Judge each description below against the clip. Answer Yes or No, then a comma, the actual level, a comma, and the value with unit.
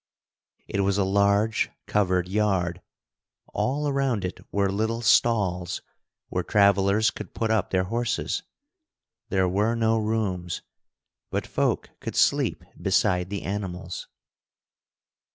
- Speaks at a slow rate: Yes, slow, 115 wpm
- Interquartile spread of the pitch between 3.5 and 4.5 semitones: No, average, 3.1 semitones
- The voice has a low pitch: Yes, low, 100 Hz